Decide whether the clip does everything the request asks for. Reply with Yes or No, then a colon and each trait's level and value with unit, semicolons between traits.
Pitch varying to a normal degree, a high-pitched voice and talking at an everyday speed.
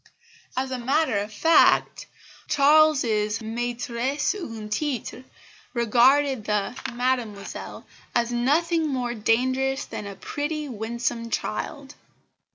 No: average, 3.9 semitones; high, 245 Hz; slow, 100 wpm